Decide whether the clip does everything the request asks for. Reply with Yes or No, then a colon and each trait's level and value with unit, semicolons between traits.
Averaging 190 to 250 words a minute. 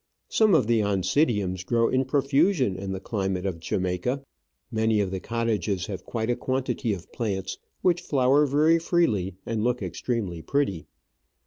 No: average, 155 wpm